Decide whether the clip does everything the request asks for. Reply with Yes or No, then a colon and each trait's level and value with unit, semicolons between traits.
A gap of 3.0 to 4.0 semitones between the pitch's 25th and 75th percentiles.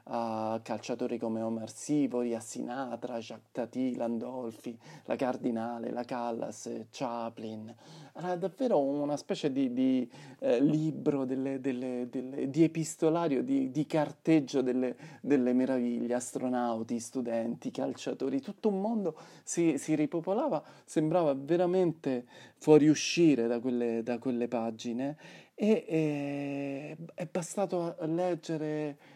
No: average, 4.9 semitones